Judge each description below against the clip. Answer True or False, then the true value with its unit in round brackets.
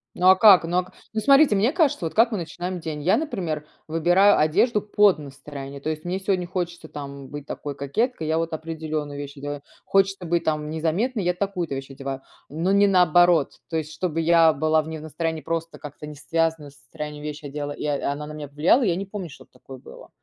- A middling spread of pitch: True (3.7 semitones)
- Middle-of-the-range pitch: True (160 Hz)